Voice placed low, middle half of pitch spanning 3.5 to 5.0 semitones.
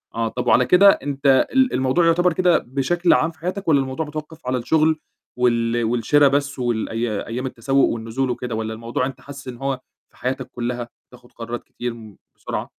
Yes: low, 130 Hz; average, 4.0 semitones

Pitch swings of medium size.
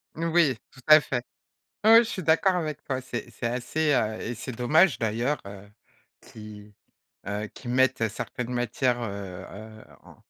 No: wide, 5.9 semitones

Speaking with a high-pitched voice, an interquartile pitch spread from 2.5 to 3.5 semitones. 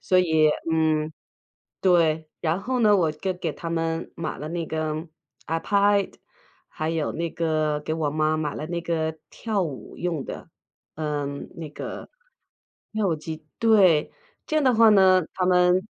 No: medium, 165 Hz; average, 3.0 semitones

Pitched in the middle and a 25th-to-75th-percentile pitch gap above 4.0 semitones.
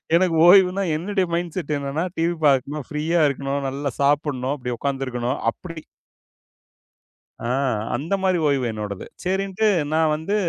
Yes: medium, 150 Hz; average, 4.5 semitones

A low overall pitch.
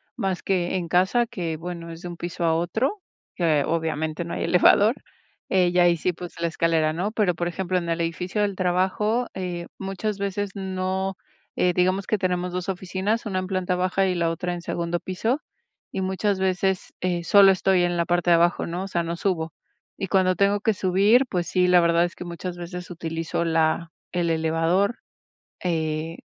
No: medium, 180 Hz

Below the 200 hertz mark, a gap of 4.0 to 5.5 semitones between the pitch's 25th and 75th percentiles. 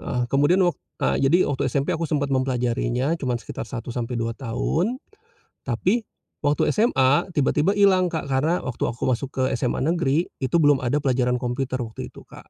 Yes: low, 135 Hz; average, 4.4 semitones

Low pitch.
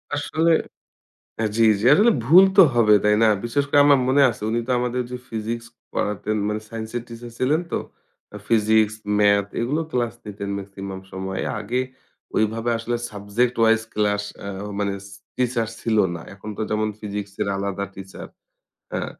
Yes: low, 110 Hz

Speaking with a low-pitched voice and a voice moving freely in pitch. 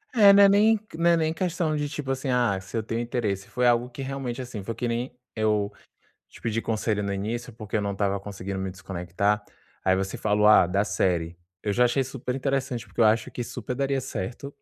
No: low, 115 Hz; average, 4.8 semitones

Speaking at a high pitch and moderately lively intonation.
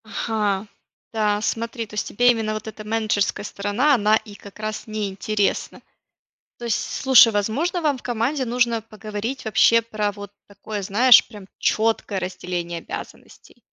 No: high, 215 Hz; narrow, 2.1 semitones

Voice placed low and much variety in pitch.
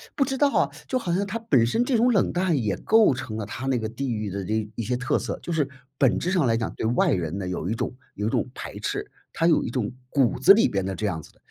Yes: low, 125 Hz; wide, 8.9 semitones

